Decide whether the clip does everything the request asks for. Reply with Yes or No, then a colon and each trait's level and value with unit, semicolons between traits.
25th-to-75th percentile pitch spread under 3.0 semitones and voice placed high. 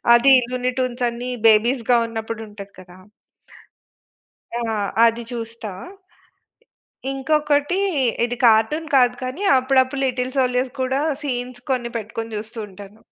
Yes: narrow, 2.4 semitones; high, 245 Hz